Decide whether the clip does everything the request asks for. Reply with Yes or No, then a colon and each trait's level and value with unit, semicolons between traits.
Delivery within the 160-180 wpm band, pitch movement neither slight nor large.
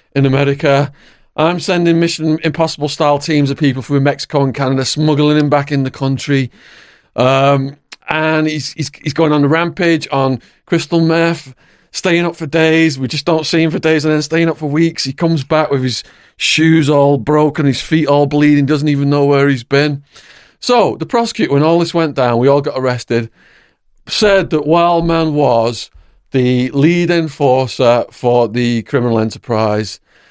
Yes: average, 175 wpm; average, 3.2 semitones